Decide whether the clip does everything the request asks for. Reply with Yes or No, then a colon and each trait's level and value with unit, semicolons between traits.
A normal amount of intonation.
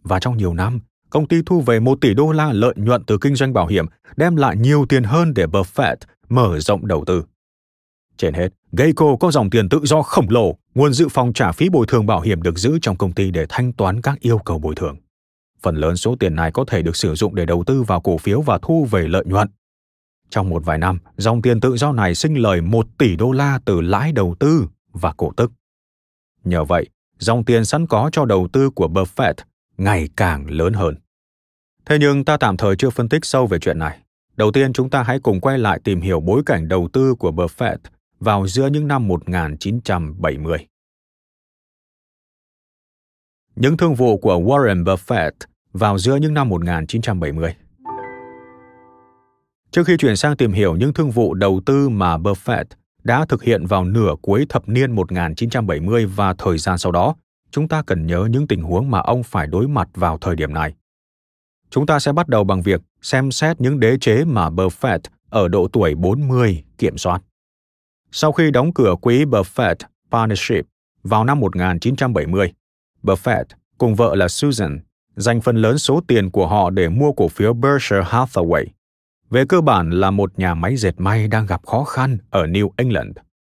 No: wide, 6.5 semitones